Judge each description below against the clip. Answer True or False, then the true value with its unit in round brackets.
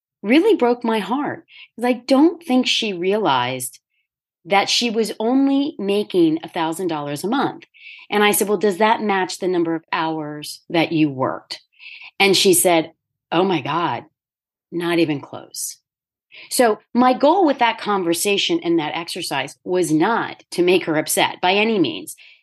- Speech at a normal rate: True (160 wpm)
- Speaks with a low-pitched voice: False (200 Hz)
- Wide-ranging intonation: True (7.1 semitones)